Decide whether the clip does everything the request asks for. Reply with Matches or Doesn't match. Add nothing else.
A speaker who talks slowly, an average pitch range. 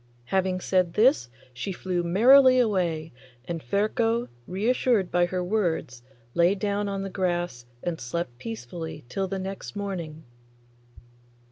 Matches